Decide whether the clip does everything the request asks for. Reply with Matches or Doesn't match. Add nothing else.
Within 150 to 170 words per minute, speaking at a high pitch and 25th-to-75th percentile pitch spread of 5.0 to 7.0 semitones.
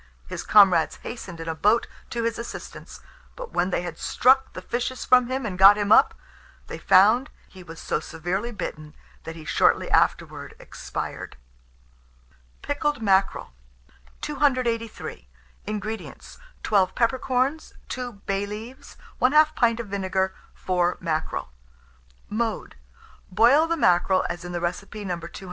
Doesn't match